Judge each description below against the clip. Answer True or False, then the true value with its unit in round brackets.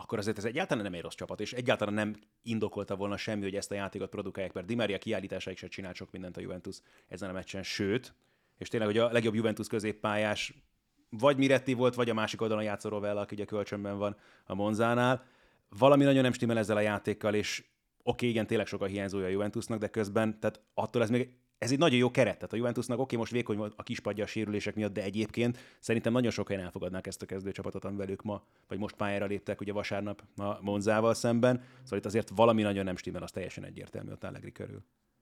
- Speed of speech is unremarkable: False (220 wpm)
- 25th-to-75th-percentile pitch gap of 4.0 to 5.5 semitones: False (2.5 semitones)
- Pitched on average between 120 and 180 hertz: False (105 Hz)